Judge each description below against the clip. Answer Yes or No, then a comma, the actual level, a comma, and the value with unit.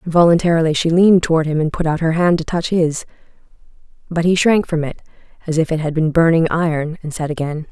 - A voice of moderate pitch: Yes, medium, 165 Hz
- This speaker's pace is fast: Yes, fast, 220 wpm